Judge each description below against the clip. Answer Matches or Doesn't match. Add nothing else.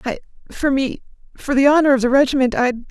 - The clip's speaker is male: Doesn't match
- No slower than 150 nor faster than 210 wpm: Matches